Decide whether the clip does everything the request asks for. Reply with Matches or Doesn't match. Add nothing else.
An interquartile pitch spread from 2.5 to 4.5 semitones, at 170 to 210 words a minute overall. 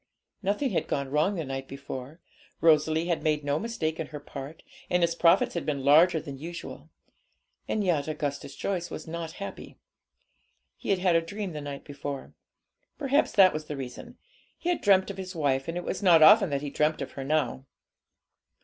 Matches